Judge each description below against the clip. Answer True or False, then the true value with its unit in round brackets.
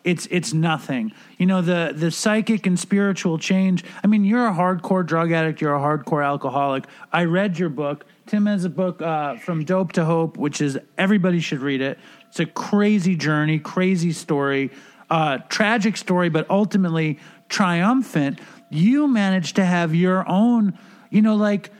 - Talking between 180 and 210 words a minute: False (170 wpm)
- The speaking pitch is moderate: True (180 Hz)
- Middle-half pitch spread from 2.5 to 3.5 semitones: False (4.3 semitones)